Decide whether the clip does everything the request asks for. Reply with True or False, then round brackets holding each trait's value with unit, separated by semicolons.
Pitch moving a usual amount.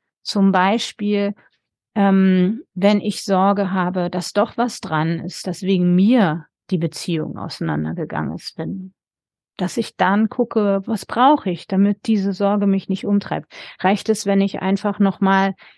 False (1.9 semitones)